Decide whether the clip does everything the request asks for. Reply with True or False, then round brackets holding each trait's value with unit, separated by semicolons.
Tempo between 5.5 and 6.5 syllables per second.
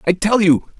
False (5.2 syllables/s)